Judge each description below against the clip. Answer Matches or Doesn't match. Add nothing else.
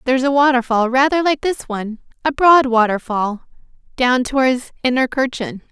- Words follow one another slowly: Matches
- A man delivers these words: Doesn't match